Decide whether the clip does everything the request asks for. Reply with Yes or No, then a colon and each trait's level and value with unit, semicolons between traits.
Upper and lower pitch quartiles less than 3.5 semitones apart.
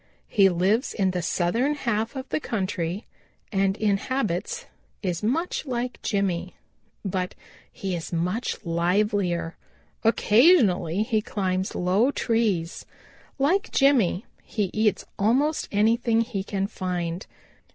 No: average, 4.3 semitones